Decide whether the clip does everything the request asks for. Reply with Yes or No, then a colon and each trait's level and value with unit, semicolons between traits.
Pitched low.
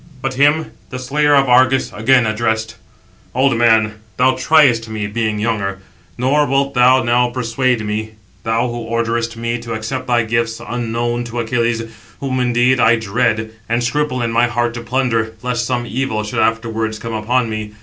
Yes: low, 120 Hz